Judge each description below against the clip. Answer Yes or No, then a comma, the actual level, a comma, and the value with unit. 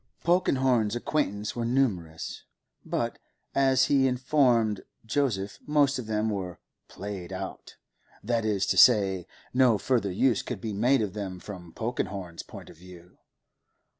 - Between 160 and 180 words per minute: No, slow, 135 wpm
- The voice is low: Yes, low, 110 Hz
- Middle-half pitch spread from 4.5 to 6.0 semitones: Yes, average, 5.0 semitones